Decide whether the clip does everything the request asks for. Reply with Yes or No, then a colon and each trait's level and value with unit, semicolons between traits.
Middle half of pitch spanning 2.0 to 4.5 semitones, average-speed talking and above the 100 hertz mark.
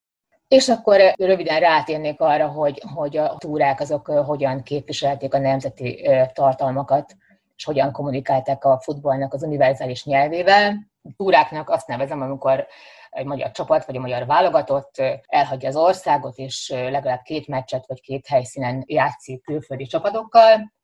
Yes: narrow, 2.5 semitones; average, 140 wpm; medium, 140 Hz